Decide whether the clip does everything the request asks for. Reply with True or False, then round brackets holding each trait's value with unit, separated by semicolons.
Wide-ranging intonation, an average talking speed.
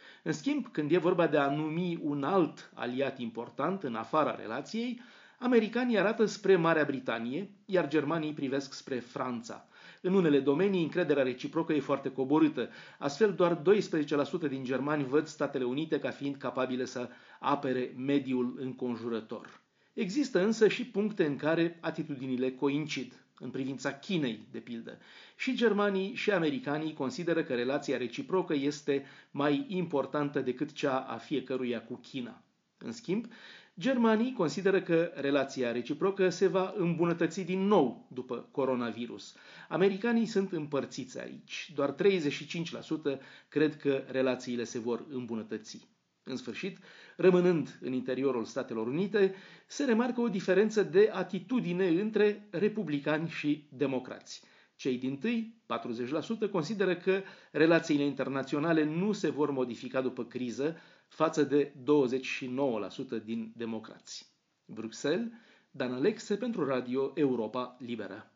True (6.4 semitones; 130 wpm)